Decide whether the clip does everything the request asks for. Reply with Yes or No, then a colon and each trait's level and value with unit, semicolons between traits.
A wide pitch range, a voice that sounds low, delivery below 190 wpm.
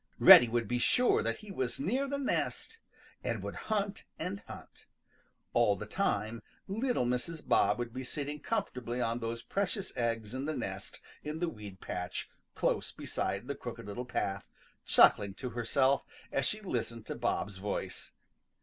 Yes: wide, 8.2 semitones; low, 125 Hz; average, 170 wpm